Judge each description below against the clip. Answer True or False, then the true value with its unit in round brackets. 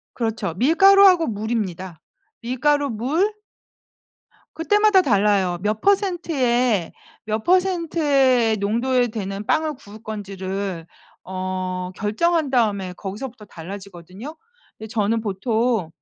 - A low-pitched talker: False (225 Hz)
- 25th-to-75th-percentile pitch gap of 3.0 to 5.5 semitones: False (6.6 semitones)